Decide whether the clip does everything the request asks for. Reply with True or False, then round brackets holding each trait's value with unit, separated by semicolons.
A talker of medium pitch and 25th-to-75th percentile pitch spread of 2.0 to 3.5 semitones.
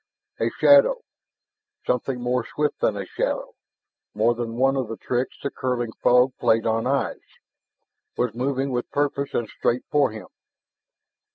False (125 Hz; 2.8 semitones)